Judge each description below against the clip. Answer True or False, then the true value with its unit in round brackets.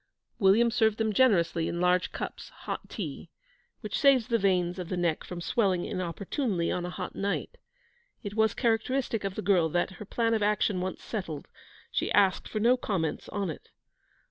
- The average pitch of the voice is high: True (195 Hz)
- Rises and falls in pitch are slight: False (3.9 semitones)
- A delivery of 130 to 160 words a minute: False (180 wpm)